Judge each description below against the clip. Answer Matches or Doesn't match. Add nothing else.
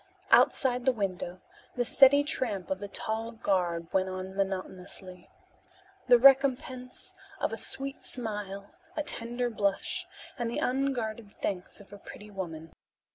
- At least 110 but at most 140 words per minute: Matches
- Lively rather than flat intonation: Doesn't match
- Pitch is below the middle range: Doesn't match